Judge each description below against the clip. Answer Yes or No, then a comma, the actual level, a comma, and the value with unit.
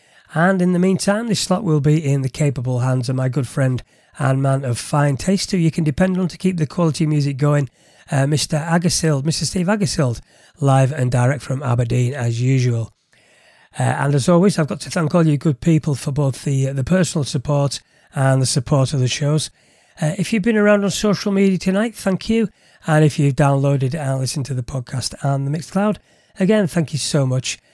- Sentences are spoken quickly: Yes, fast, 210 wpm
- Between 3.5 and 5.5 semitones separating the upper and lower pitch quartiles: Yes, average, 4.7 semitones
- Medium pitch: Yes, medium, 150 Hz